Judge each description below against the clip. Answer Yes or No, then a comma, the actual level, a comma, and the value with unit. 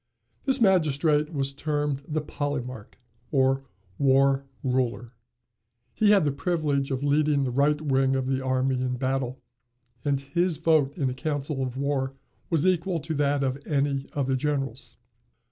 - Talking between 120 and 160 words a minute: Yes, average, 155 wpm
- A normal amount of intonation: No, narrow, 2.1 semitones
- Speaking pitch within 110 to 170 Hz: Yes, medium, 140 Hz